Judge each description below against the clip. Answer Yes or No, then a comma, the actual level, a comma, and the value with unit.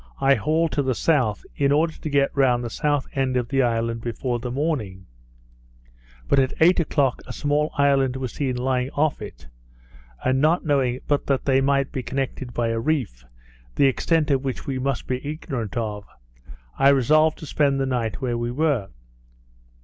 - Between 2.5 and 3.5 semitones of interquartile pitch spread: Yes, average, 2.9 semitones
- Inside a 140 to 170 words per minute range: No, average, 180 wpm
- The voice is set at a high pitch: No, low, 135 Hz